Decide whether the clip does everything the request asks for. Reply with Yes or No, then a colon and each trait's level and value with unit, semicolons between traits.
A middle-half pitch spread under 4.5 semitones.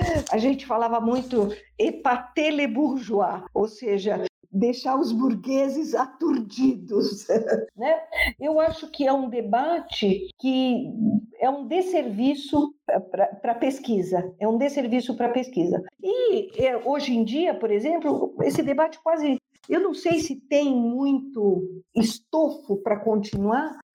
No: average, 5.3 semitones